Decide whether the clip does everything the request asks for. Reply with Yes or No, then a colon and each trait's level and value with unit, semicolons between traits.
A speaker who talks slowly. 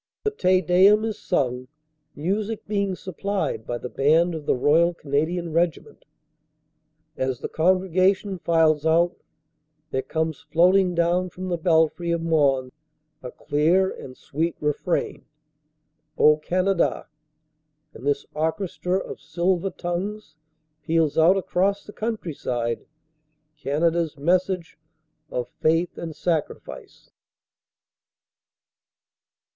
Yes: slow, 110 wpm